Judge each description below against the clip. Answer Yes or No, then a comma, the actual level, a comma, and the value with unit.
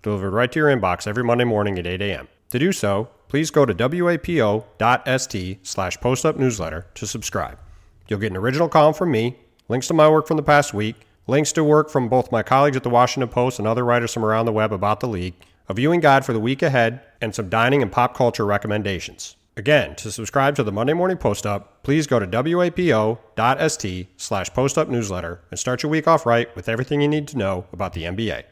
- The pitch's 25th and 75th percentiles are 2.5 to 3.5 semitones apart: No, average, 5.2 semitones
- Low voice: Yes, low, 115 Hz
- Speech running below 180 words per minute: No, fast, 205 wpm